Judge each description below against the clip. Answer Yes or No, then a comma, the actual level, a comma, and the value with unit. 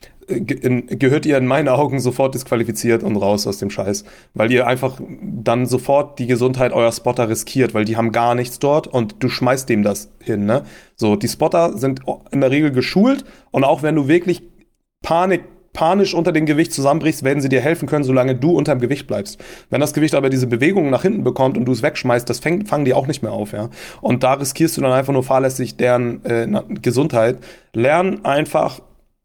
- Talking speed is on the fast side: Yes, fast, 205 wpm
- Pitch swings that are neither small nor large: Yes, average, 3.6 semitones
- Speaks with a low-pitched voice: Yes, low, 130 Hz